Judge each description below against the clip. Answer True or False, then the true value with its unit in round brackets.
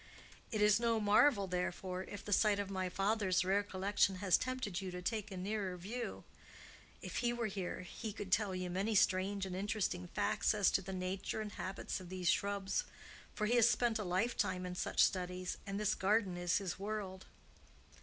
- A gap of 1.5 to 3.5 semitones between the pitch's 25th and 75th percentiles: True (2.4 semitones)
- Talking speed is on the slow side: False (195 wpm)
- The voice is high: True (195 Hz)